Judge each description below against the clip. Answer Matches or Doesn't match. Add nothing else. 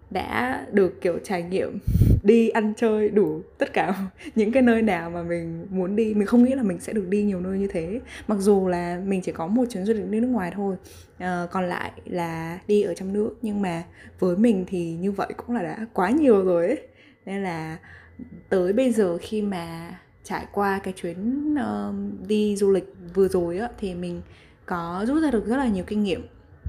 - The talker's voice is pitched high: Matches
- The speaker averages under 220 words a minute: Matches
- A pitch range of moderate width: Matches